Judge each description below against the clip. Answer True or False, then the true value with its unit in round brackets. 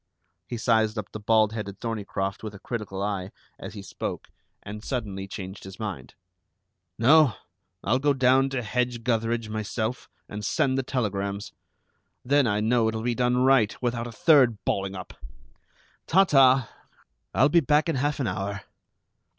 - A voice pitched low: True (115 Hz)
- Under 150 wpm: False (160 wpm)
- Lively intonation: False (3.8 semitones)